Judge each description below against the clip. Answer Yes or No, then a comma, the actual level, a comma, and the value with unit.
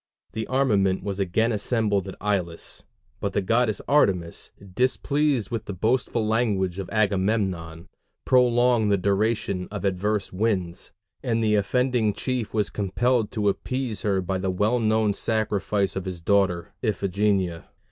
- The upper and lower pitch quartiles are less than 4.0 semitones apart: Yes, average, 3.0 semitones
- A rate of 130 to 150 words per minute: Yes, average, 140 wpm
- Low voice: Yes, low, 105 Hz